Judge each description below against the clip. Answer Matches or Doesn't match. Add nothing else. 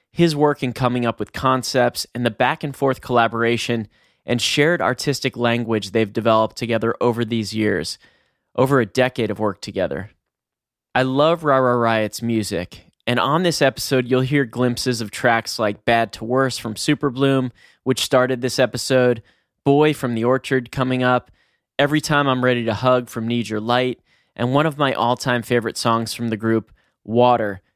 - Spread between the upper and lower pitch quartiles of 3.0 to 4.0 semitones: Doesn't match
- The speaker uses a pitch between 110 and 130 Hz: Matches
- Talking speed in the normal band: Matches